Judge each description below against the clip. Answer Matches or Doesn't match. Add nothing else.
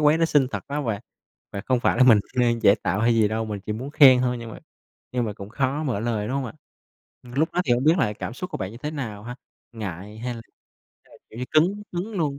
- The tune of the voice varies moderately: Matches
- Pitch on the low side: Matches